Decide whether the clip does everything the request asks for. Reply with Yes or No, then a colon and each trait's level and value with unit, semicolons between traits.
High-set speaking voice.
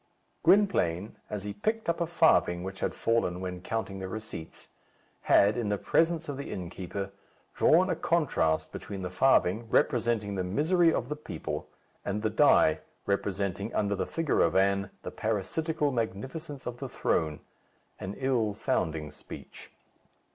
No: low, 105 Hz